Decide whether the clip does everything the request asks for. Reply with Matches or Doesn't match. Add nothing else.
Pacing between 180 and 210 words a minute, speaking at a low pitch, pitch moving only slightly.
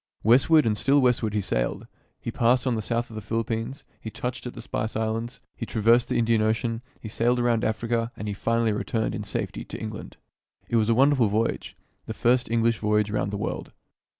Matches